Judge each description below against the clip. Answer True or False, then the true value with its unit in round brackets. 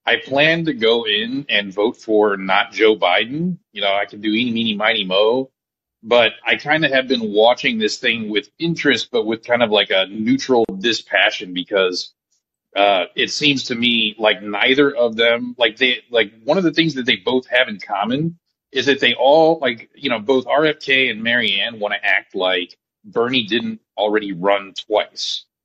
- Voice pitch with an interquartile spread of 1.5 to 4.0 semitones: False (5.0 semitones)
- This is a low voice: True (120 Hz)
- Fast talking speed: False (190 wpm)